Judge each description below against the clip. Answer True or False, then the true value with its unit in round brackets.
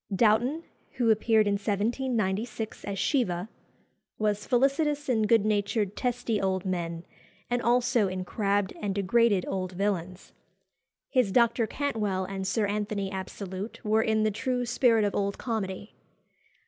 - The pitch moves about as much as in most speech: True (3.4 semitones)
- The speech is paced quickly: False (135 wpm)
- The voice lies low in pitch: False (210 Hz)